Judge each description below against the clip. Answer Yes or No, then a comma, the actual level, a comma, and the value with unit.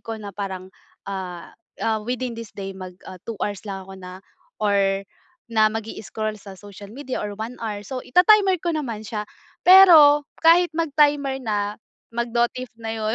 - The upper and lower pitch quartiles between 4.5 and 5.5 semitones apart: Yes, average, 4.9 semitones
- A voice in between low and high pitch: No, high, 220 Hz